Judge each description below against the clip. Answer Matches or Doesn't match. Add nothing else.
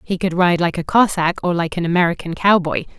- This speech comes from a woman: Matches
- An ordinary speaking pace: Doesn't match